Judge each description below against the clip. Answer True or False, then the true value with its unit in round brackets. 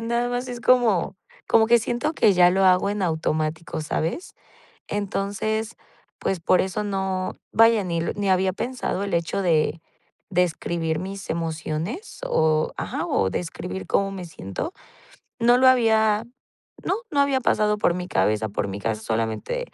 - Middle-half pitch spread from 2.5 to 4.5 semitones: False (5.3 semitones)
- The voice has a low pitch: False (190 Hz)